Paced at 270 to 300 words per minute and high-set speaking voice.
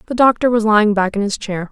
Yes: fast, 280 wpm; high, 215 Hz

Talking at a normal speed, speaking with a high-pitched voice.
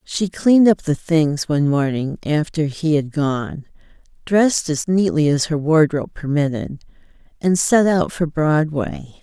No: average, 150 wpm; medium, 155 Hz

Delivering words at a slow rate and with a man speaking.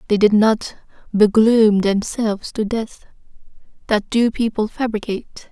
No: slow, 110 wpm; female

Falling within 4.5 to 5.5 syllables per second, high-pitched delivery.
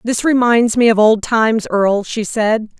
Yes: 4.6 syllables/s; high, 225 Hz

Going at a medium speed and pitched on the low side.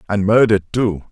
Yes: average, 160 wpm; low, 105 Hz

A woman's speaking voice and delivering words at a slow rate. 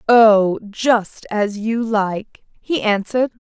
Yes: female; slow, 120 wpm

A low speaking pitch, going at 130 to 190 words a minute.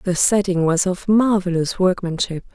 No: medium, 185 Hz; average, 140 wpm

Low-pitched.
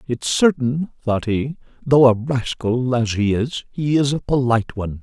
Yes: low, 125 Hz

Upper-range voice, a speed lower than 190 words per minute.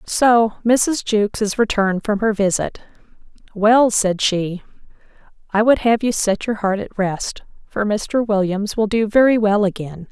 Yes: high, 210 Hz; average, 165 wpm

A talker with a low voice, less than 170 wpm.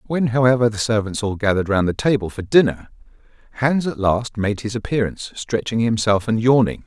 No: low, 115 Hz; average, 185 wpm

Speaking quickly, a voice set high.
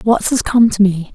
Yes: fast, 260 wpm; high, 210 Hz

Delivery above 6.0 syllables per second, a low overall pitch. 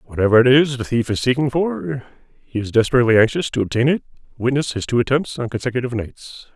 Yes: 6.4 syllables/s; low, 125 Hz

